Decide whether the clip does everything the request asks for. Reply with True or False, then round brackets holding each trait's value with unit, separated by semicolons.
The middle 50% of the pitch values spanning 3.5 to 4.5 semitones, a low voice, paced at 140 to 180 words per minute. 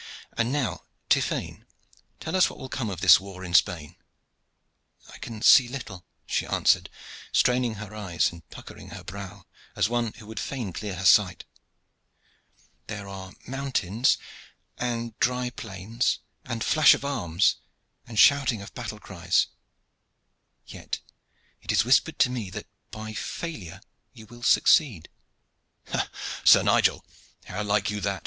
True (4.2 semitones; 110 Hz; 145 wpm)